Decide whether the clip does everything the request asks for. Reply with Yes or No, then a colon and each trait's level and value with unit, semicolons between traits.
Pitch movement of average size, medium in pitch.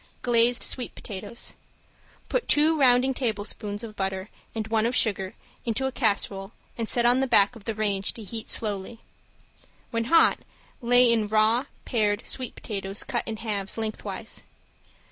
No: average, 3.0 semitones; high, 225 Hz